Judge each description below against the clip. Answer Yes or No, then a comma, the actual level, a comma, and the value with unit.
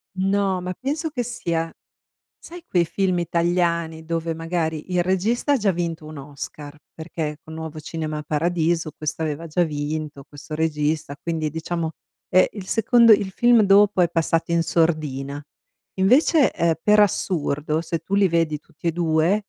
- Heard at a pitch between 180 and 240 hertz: No, medium, 165 Hz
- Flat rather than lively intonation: No, average, 3.3 semitones